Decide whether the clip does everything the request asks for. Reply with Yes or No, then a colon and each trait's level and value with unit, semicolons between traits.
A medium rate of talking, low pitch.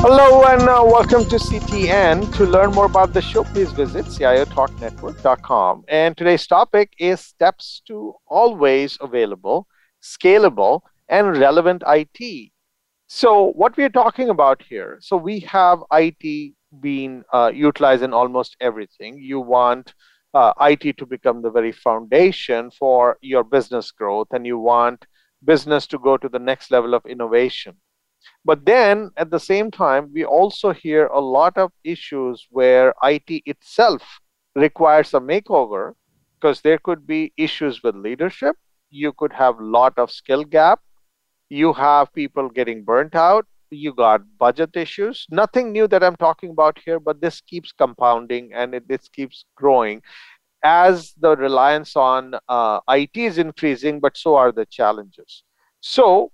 No: average, 150 wpm; medium, 150 Hz